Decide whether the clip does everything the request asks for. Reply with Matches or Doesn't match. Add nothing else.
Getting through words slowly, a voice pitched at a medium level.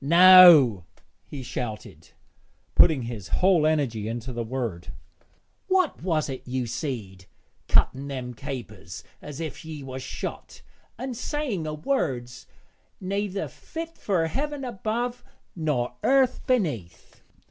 Matches